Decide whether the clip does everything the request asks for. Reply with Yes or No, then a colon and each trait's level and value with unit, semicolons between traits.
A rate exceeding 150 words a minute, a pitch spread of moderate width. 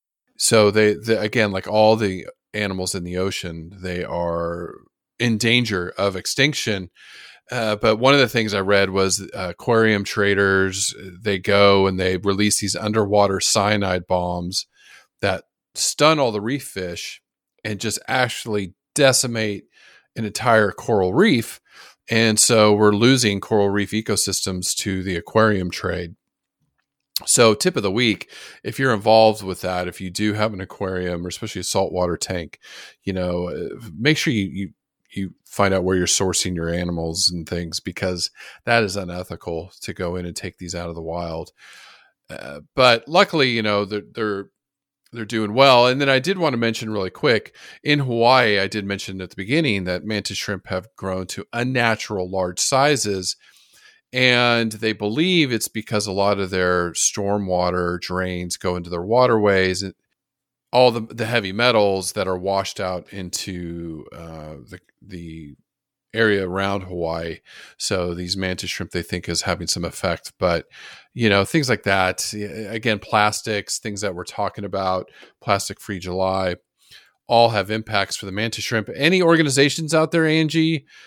Yes: average, 165 wpm; average, 3.5 semitones